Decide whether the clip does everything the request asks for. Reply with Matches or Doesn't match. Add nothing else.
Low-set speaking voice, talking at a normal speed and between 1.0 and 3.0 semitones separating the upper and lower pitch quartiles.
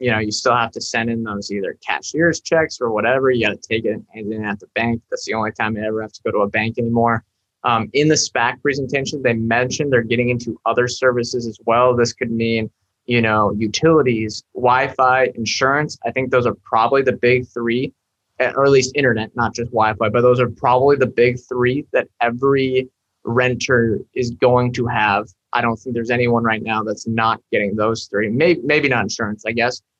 Doesn't match